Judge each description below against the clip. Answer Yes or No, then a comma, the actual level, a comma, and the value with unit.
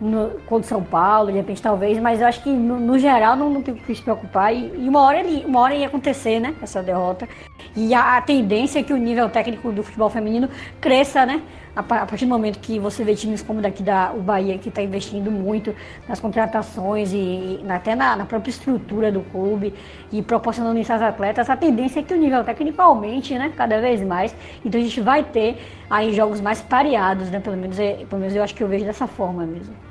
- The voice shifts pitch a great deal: No, average, 3.4 semitones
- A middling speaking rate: No, fast, 230 wpm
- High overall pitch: Yes, high, 225 Hz